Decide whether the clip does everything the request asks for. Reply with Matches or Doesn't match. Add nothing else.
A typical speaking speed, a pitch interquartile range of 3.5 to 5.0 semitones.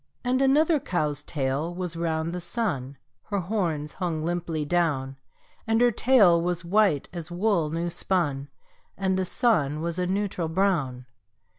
Matches